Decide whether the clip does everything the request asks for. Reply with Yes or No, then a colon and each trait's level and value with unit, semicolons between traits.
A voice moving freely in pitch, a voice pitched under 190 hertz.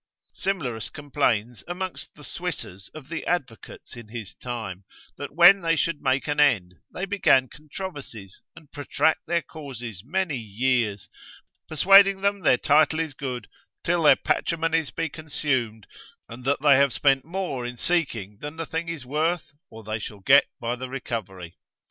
Yes: wide, 5.7 semitones; medium, 140 Hz